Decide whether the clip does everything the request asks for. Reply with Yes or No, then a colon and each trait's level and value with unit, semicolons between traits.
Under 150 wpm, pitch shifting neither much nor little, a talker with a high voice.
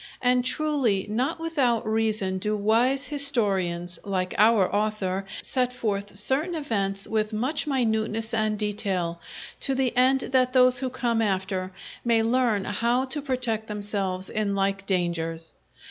Yes: average, 140 wpm; average, 4.3 semitones; high, 220 Hz